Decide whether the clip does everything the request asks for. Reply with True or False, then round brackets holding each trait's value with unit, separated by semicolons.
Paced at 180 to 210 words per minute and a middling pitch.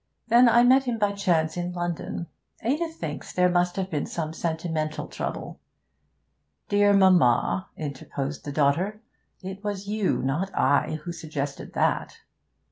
False (140 wpm; 175 Hz)